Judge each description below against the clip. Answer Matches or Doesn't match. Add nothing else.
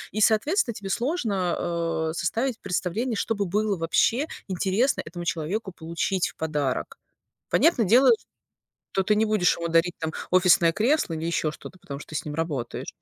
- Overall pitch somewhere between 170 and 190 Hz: Matches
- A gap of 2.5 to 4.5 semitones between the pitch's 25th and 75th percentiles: Doesn't match